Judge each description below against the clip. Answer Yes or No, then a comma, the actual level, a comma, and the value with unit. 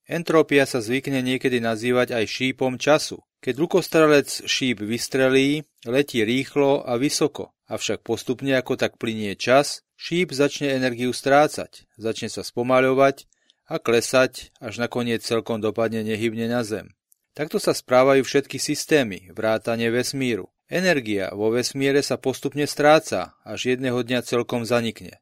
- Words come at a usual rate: Yes, average, 135 wpm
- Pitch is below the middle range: Yes, low, 130 Hz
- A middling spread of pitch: Yes, average, 3.3 semitones